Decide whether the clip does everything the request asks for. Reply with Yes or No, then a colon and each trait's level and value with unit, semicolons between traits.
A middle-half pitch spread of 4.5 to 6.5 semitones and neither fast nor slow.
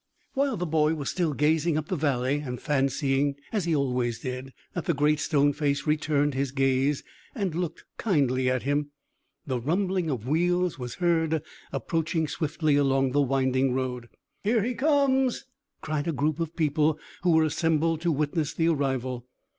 No: average, 3.4 semitones; average, 170 wpm